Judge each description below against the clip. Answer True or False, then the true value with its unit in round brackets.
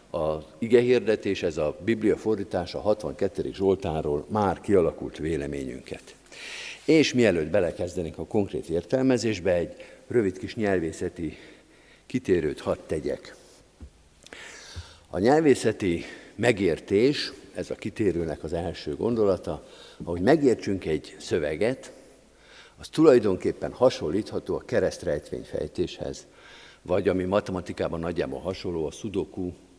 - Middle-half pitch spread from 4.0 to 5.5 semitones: True (5.2 semitones)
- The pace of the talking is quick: False (105 wpm)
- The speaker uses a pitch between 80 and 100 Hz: True (95 Hz)